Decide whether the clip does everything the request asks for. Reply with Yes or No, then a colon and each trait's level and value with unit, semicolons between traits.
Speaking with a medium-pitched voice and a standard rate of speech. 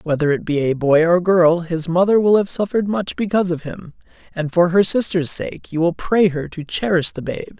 No: medium, 175 Hz; fast, 230 wpm